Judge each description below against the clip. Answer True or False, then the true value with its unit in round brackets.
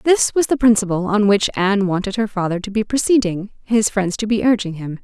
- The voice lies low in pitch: False (210 Hz)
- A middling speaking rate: False (225 wpm)